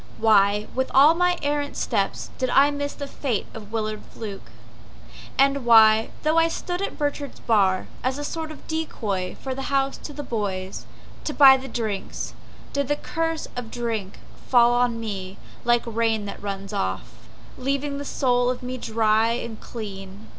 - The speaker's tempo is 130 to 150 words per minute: No, average, 175 wpm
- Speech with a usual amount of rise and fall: Yes, average, 4.7 semitones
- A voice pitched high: Yes, high, 240 Hz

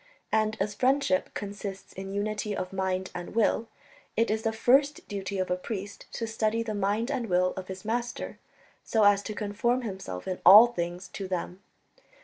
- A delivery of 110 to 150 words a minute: No, average, 180 wpm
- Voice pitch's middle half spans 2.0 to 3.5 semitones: Yes, average, 3.0 semitones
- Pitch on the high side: Yes, high, 205 Hz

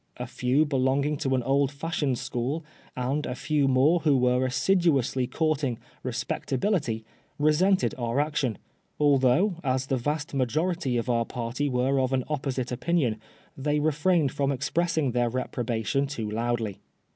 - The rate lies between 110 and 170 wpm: Yes, average, 150 wpm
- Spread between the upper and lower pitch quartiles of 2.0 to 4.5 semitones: Yes, average, 3.2 semitones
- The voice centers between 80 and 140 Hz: Yes, low, 135 Hz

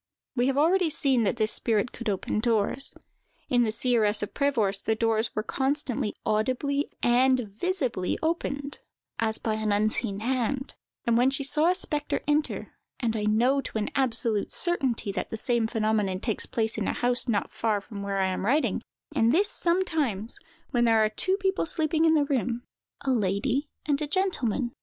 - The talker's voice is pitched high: Yes, high, 240 Hz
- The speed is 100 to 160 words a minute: No, average, 175 wpm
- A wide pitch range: No, average, 4.6 semitones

